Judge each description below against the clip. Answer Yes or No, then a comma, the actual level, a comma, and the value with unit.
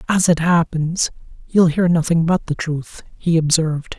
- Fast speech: No, average, 165 wpm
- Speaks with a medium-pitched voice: Yes, medium, 165 Hz